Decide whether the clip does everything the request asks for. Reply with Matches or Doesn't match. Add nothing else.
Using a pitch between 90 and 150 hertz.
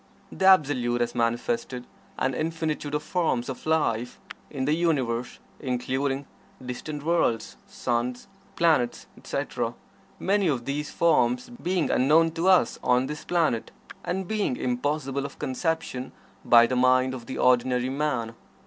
Matches